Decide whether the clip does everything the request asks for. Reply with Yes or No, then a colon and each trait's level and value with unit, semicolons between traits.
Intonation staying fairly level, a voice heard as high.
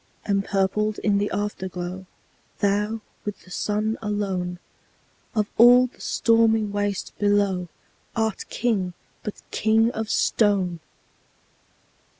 Yes: narrow, 2.3 semitones; high, 205 Hz